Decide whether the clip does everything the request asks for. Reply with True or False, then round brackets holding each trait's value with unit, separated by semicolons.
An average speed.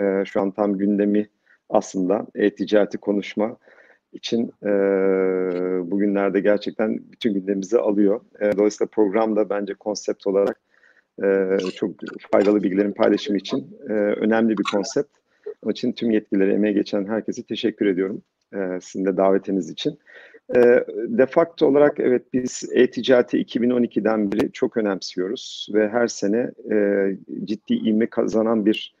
True (130 wpm)